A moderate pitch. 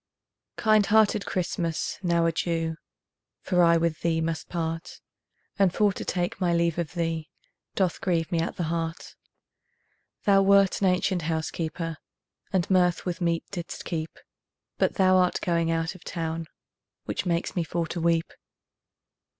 Yes: medium, 170 Hz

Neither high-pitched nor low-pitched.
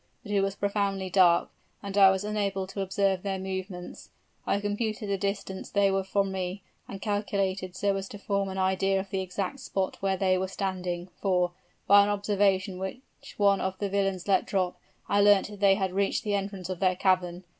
No: high, 195 Hz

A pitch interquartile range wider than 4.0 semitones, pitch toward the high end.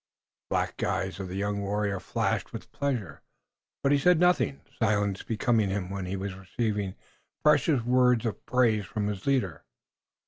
No: average, 4.4 semitones; low, 105 Hz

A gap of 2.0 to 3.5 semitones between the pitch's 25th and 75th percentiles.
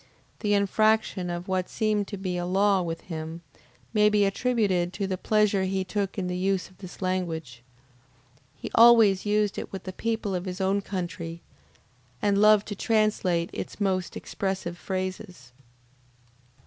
Yes: narrow, 2.4 semitones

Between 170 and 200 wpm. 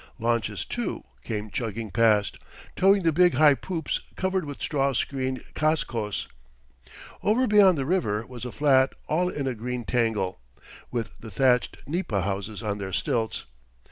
No: average, 150 wpm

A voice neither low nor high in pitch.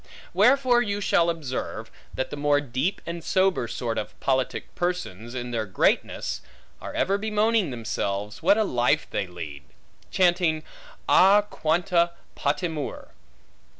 Yes: medium, 160 Hz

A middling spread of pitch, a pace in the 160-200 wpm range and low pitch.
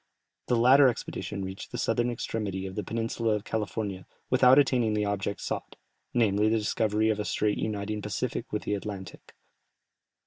No: narrow, 2.1 semitones; average, 170 wpm; low, 105 Hz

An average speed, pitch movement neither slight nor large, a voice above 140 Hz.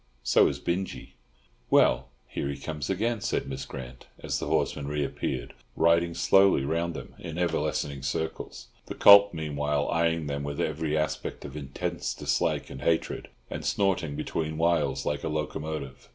No: average, 160 wpm; average, 3.0 semitones; very low, 75 Hz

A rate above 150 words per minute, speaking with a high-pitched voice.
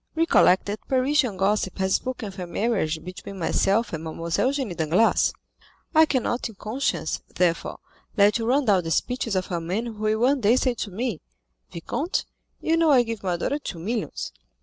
Yes: average, 185 wpm; high, 215 Hz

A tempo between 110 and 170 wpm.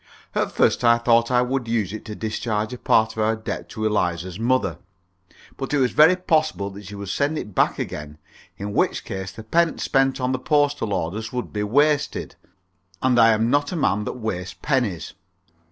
No: average, 200 wpm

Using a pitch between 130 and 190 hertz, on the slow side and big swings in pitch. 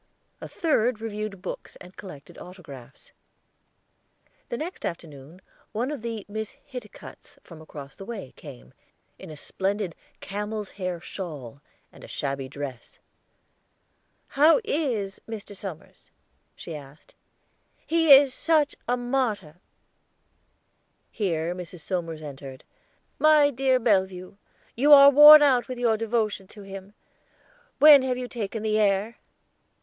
No: high, 205 Hz; slow, 125 wpm; wide, 6.7 semitones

